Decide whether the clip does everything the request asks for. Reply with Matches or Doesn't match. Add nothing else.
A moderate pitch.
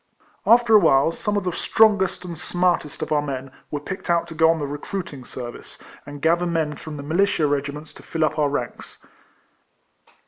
Matches